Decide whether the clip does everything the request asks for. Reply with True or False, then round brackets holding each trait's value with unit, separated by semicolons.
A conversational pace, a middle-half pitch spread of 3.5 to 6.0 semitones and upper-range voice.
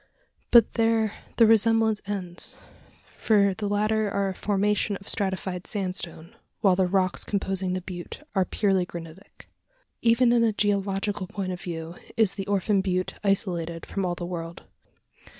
False (150 wpm; 2.5 semitones; 195 Hz)